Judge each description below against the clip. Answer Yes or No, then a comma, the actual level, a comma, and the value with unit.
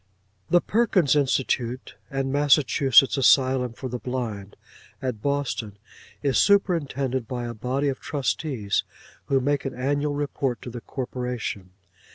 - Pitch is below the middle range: Yes, low, 130 Hz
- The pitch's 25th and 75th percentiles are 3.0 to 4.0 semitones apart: No, narrow, 2.6 semitones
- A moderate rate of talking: No, slow, 130 wpm